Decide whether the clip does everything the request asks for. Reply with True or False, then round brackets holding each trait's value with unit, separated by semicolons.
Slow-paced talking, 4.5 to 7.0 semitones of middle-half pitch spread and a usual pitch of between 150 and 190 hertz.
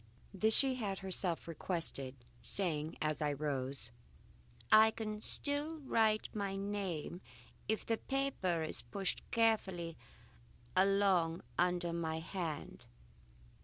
True (110 wpm; 4.8 semitones; 185 Hz)